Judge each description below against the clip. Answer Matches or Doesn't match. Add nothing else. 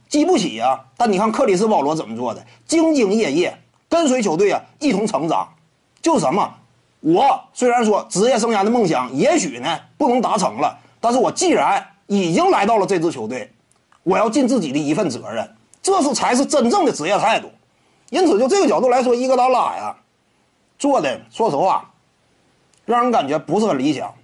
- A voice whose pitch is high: Matches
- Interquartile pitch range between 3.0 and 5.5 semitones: Matches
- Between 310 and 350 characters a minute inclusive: Doesn't match